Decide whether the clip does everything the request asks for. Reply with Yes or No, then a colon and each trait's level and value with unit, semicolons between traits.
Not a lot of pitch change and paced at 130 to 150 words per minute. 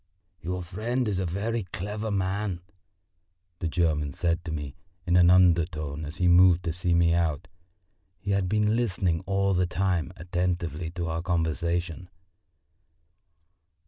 Yes: narrow, 2.3 semitones; average, 140 wpm